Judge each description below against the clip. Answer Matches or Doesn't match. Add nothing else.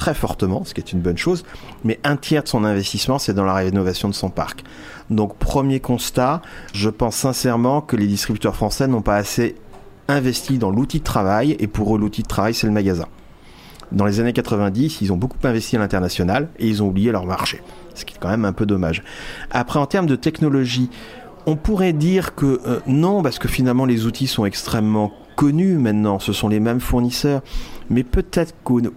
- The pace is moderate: Matches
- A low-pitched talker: Matches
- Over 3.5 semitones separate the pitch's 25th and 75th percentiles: Matches